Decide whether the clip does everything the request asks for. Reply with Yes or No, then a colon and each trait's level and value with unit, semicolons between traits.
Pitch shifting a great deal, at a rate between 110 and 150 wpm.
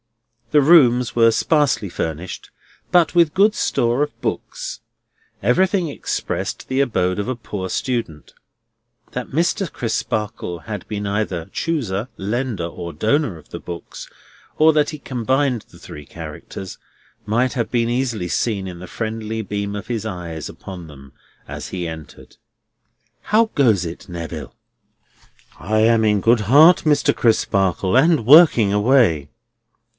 Yes: wide, 6.1 semitones; average, 140 wpm